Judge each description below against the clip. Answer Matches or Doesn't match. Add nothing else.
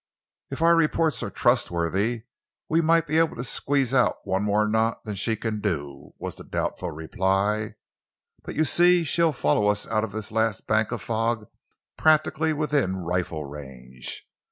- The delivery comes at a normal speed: Matches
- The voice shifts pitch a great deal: Matches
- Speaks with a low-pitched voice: Matches